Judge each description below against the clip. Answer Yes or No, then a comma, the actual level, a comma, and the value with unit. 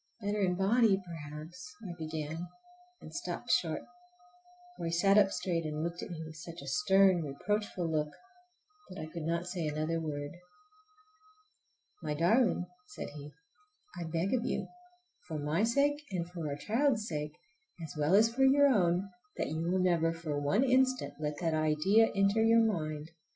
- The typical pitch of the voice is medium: Yes, medium, 170 Hz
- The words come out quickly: No, average, 165 wpm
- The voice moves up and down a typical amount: Yes, average, 4.6 semitones